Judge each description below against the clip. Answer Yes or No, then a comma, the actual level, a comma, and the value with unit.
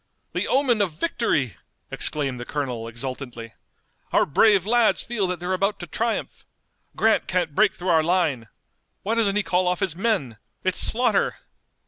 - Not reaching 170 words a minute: Yes, average, 160 wpm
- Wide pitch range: Yes, wide, 7.3 semitones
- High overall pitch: No, medium, 180 Hz